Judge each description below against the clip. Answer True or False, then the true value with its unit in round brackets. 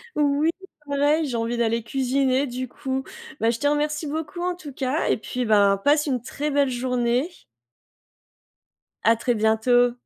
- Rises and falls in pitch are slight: False (3.6 semitones)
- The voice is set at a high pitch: True (260 Hz)